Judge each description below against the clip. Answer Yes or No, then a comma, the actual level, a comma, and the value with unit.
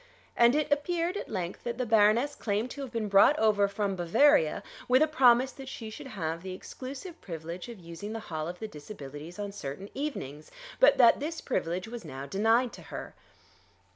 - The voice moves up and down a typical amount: No, wide, 6.7 semitones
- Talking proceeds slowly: No, average, 195 wpm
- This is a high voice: Yes, high, 215 Hz